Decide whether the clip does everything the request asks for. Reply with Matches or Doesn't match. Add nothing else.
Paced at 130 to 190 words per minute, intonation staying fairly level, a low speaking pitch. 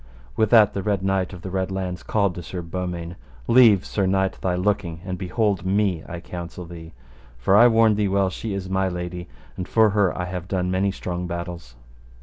Doesn't match